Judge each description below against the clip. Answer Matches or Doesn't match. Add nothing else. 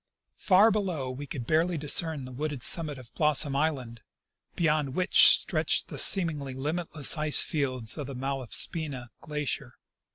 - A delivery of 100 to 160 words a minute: Matches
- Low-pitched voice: Doesn't match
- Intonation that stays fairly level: Doesn't match